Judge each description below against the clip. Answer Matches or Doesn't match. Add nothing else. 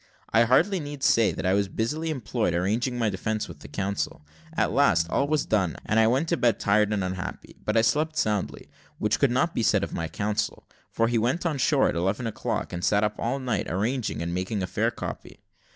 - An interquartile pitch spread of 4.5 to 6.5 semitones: Matches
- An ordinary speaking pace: Doesn't match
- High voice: Doesn't match